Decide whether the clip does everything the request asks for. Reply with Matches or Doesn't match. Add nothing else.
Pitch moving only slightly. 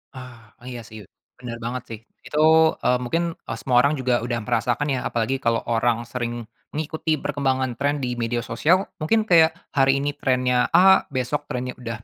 Doesn't match